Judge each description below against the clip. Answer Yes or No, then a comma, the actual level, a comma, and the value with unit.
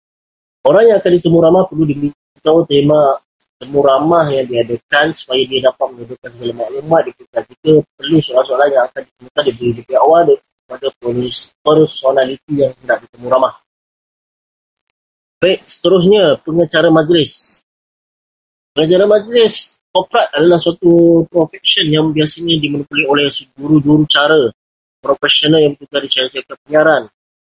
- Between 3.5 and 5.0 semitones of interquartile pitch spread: Yes, average, 4.0 semitones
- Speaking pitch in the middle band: Yes, medium, 150 Hz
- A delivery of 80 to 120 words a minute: No, average, 130 wpm